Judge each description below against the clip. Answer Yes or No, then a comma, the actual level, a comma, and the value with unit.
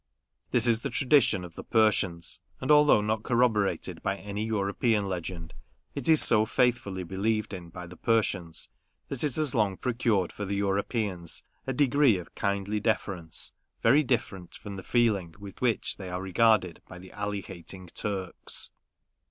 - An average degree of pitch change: Yes, average, 3.7 semitones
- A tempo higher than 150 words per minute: Yes, average, 160 wpm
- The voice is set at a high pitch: No, low, 100 Hz